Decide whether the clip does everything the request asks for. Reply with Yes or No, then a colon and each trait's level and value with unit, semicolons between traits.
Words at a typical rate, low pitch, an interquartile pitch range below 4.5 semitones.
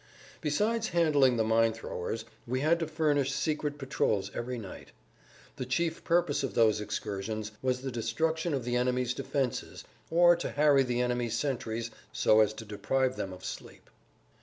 No: average, 160 wpm; low, 125 Hz; average, 4.8 semitones